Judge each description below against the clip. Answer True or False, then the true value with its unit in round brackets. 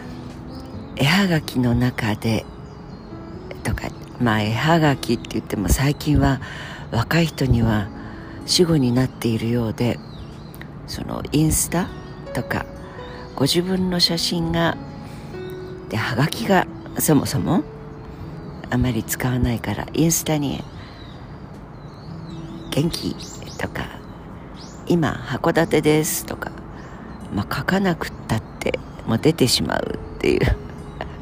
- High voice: False (140 Hz)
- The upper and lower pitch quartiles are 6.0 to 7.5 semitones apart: False (5.6 semitones)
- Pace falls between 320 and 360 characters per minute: False (190 characters per minute)